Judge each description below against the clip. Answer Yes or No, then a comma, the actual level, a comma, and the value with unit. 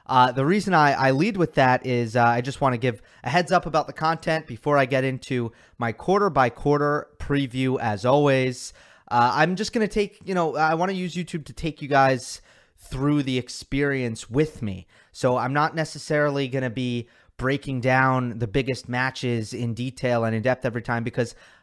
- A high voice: No, low, 135 Hz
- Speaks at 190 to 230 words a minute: Yes, fast, 205 wpm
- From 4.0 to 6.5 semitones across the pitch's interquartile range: No, average, 3.3 semitones